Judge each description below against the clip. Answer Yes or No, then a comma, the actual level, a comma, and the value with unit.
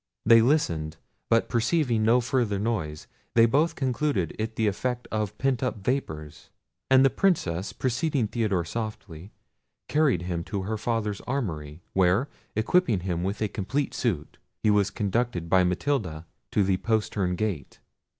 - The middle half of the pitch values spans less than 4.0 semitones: No, average, 5.3 semitones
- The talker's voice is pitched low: Yes, low, 110 Hz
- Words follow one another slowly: No, average, 150 wpm